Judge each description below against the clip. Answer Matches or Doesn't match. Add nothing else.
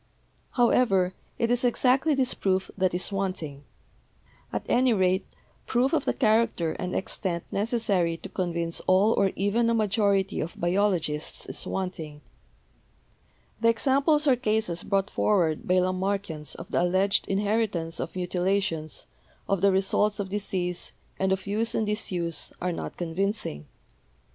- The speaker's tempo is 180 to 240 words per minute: Doesn't match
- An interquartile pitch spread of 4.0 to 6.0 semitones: Doesn't match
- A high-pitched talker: Matches